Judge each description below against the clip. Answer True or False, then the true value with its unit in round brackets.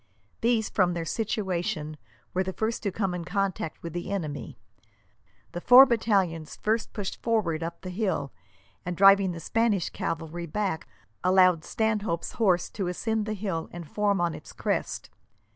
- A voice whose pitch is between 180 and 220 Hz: True (185 Hz)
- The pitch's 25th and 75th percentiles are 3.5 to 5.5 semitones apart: True (3.9 semitones)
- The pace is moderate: True (160 wpm)